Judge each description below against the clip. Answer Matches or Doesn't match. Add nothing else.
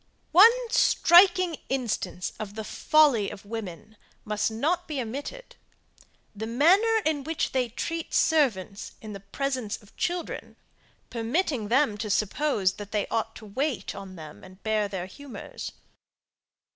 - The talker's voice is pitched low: Doesn't match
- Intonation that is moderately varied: Doesn't match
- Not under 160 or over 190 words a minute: Doesn't match